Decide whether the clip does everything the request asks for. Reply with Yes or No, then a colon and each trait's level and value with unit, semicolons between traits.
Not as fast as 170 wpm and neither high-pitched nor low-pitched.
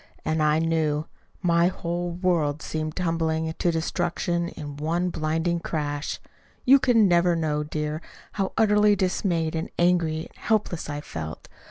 Yes: average, 145 wpm; medium, 165 Hz